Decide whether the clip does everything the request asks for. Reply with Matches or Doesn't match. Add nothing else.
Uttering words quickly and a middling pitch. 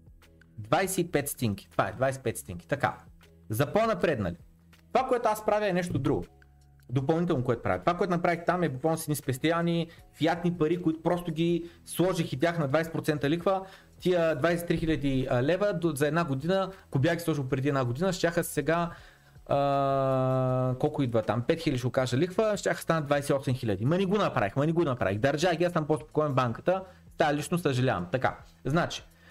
Matches